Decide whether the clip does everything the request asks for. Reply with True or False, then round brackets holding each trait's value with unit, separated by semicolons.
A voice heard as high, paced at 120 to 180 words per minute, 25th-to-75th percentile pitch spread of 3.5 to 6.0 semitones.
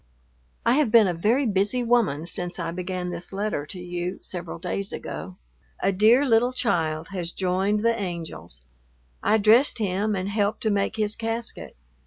True (200 Hz; 170 wpm; 4.0 semitones)